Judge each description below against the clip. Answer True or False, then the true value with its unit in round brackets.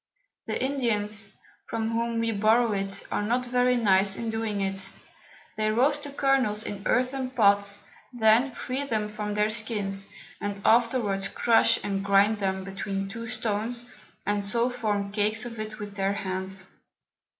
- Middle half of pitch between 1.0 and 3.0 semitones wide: True (2.7 semitones)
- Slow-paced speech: False (155 wpm)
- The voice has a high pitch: True (215 Hz)